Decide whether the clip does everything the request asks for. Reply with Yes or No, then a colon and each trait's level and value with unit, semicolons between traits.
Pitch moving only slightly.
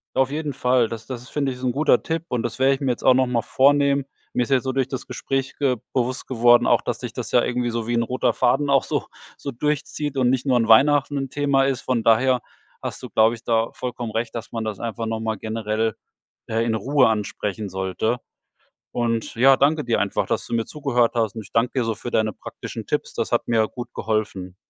No: average, 3.1 semitones